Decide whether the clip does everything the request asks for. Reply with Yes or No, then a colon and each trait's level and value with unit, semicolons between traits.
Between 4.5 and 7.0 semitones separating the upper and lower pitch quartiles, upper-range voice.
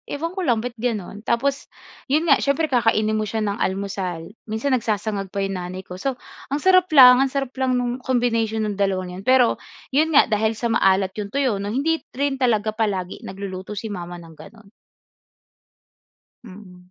Yes: average, 4.8 semitones; high, 220 Hz